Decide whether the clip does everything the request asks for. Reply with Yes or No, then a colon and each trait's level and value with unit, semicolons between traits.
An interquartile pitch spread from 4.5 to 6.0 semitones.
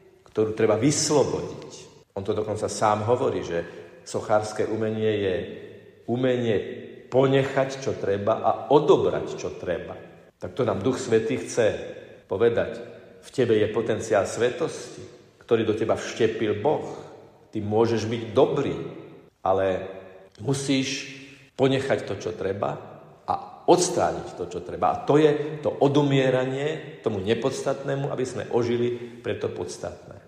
Yes: average, 5.0 semitones